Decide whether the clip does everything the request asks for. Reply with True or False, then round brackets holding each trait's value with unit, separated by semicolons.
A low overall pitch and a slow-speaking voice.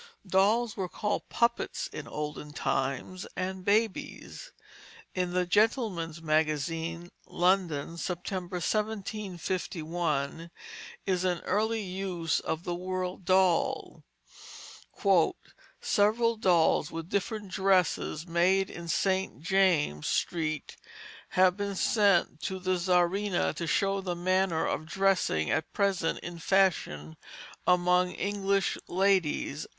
False (180 Hz; 105 wpm)